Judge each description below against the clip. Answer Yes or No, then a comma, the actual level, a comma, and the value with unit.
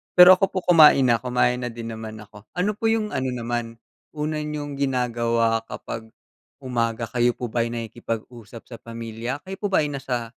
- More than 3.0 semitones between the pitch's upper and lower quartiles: Yes, average, 4.0 semitones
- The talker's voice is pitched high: No, low, 120 Hz